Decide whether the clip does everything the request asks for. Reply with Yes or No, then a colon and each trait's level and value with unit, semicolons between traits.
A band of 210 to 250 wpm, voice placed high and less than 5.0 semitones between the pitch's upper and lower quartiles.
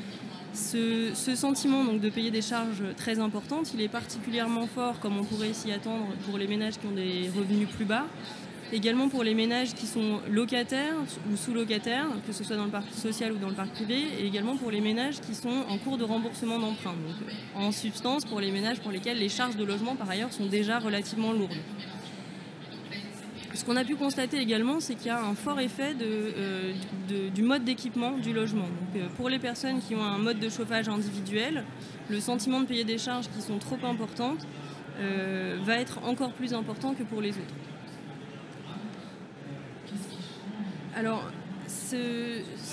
No: average, 190 wpm; high, 220 Hz; average, 2.9 semitones